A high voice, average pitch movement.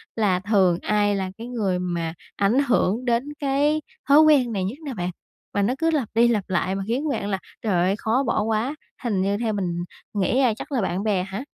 Yes: high, 215 Hz; average, 4.6 semitones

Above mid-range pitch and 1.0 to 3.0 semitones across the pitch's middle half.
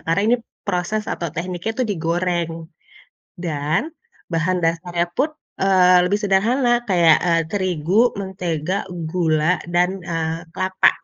No: medium, 180 Hz; narrow, 2.6 semitones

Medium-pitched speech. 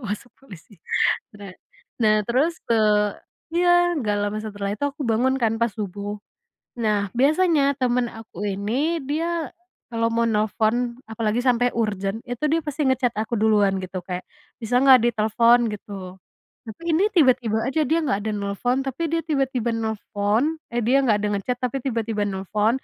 No: high, 230 Hz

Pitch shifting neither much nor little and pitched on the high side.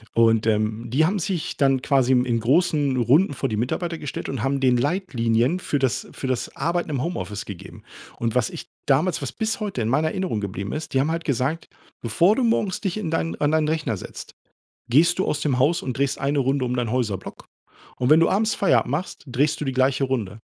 No: average, 5.0 semitones; low, 135 Hz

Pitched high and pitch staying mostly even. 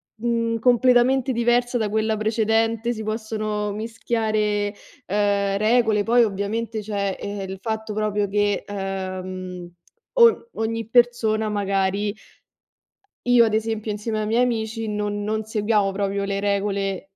Yes: high, 215 Hz; narrow, 1.9 semitones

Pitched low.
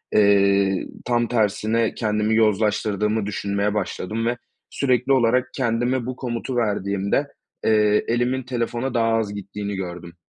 Yes: low, 110 Hz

